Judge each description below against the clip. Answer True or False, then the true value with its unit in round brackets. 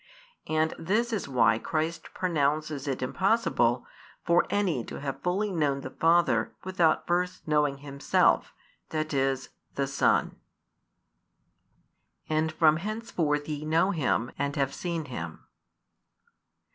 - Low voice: False (155 Hz)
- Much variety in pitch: False (3.9 semitones)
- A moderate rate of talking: False (120 wpm)